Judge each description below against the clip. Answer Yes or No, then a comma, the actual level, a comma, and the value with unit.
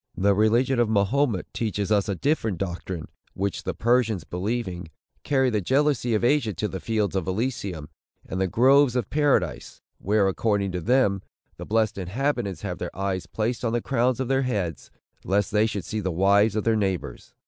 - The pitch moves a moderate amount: Yes, average, 4.2 semitones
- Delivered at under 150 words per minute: No, average, 185 wpm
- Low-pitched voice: Yes, low, 105 Hz